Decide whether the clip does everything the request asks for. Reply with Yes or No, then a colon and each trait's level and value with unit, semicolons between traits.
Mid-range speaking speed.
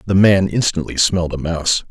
Yes: average, 190 wpm